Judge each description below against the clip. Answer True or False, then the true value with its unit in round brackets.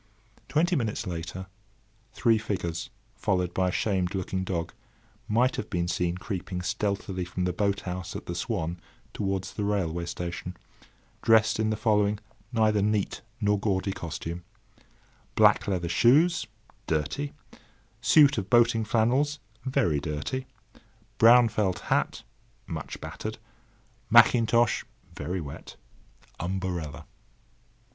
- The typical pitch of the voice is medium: False (95 Hz)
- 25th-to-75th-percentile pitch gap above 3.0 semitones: True (4.2 semitones)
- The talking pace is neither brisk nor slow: False (120 wpm)